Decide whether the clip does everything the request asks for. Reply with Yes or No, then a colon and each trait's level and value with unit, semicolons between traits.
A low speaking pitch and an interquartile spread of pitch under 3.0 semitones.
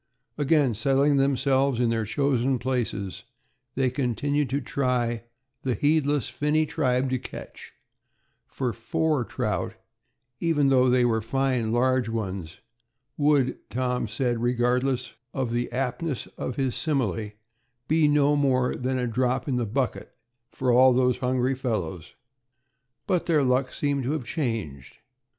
Yes: low, 130 Hz; narrow, 2.6 semitones